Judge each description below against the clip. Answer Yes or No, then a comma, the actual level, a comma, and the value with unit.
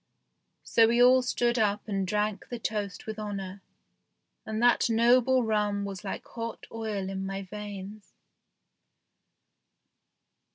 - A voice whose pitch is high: Yes, high, 210 Hz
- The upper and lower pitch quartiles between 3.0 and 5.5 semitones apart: No, narrow, 2.5 semitones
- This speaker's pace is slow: Yes, slow, 125 wpm